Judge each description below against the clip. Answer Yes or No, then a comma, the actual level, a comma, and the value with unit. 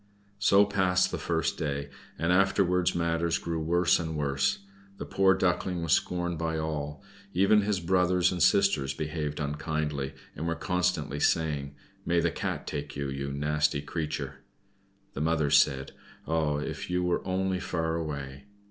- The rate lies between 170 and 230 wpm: No, average, 155 wpm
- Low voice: Yes, very low, 80 Hz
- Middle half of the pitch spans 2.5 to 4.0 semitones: Yes, average, 3.7 semitones